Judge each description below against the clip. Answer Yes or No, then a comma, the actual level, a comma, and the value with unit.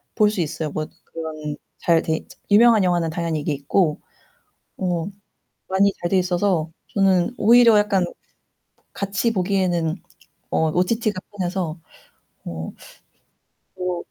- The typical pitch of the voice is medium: Yes, medium, 180 Hz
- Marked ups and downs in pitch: No, average, 3.6 semitones